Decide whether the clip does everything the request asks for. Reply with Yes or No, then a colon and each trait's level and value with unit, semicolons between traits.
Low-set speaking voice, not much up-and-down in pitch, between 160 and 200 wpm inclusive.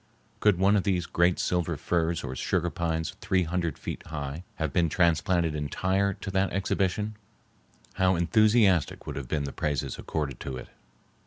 No: very low, 85 Hz; average, 3.4 semitones; average, 165 wpm